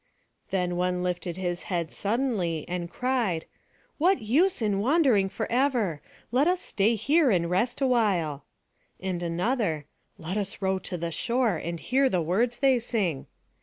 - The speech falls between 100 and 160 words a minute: Yes, average, 150 wpm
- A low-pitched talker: No, high, 200 Hz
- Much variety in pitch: Yes, wide, 6.0 semitones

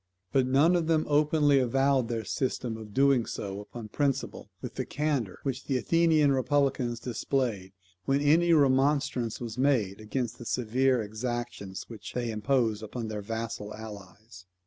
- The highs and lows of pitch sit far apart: No, average, 4.1 semitones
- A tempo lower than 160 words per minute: Yes, average, 150 wpm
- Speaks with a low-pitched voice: Yes, low, 125 Hz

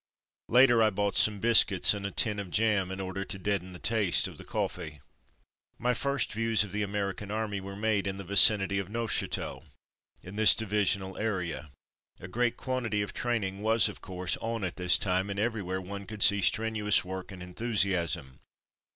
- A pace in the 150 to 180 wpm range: No, average, 195 wpm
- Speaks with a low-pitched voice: Yes, low, 100 Hz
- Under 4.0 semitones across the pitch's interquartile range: Yes, average, 2.8 semitones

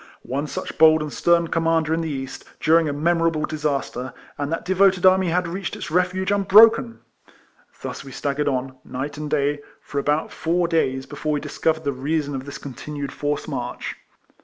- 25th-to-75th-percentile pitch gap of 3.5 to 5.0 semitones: No, average, 3.0 semitones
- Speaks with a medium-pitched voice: Yes, medium, 155 Hz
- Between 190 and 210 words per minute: No, average, 180 wpm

